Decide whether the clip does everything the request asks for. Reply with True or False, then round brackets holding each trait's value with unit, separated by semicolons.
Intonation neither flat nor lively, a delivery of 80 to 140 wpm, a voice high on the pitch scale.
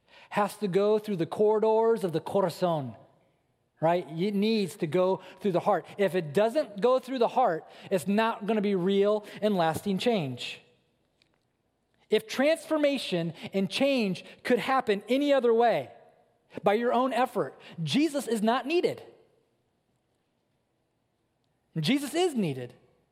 False (6.1 semitones; 135 wpm; 205 Hz)